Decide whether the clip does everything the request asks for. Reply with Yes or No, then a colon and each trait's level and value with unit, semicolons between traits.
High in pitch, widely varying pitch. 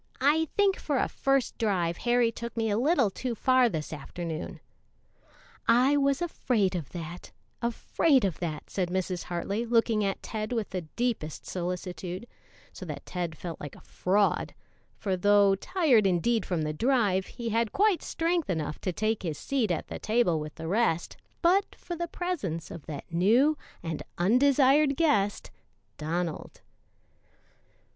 Yes: high, 210 Hz; wide, 6.7 semitones